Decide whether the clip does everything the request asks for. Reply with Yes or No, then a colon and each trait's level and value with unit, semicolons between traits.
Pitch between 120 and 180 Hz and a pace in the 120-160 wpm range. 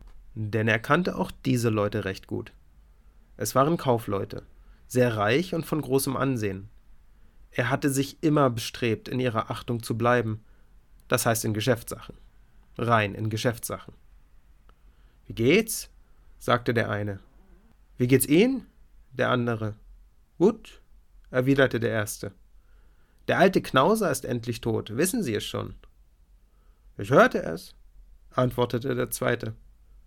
No: low, 110 Hz; average, 130 wpm